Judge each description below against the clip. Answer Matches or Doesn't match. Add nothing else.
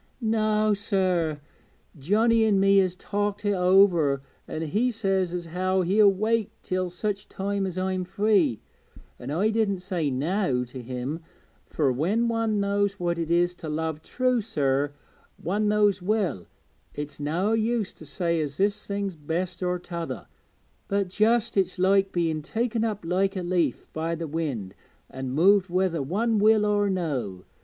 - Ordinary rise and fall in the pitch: Matches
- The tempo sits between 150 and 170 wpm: Matches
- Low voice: Doesn't match